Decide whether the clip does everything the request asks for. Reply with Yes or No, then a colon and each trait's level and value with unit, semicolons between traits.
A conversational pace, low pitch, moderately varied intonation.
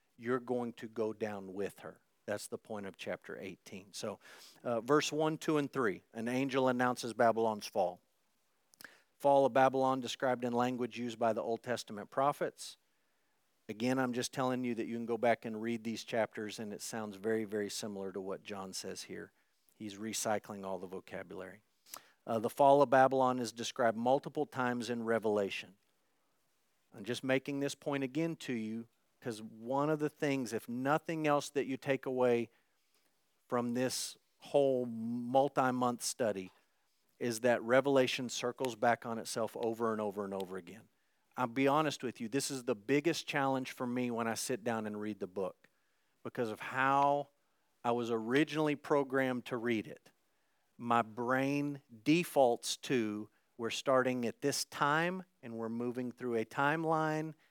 Yes: average, 170 wpm; low, 125 Hz; average, 3.0 semitones